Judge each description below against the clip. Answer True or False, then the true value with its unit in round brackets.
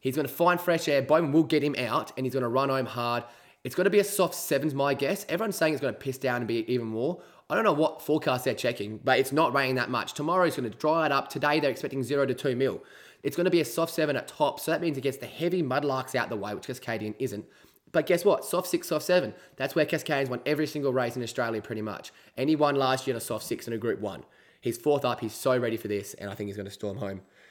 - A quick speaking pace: True (295 wpm)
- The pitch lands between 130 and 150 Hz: True (135 Hz)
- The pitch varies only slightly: False (4.2 semitones)